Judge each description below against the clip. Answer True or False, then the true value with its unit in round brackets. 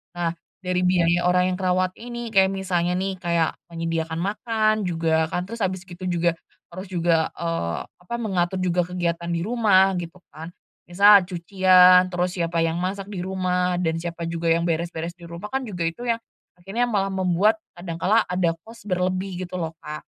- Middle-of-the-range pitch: True (180 Hz)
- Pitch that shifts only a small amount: True (2.0 semitones)